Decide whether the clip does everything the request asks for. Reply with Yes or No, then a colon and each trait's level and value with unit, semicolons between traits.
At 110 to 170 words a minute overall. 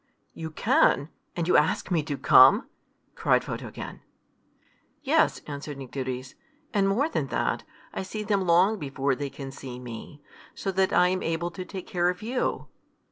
Yes: average, 165 wpm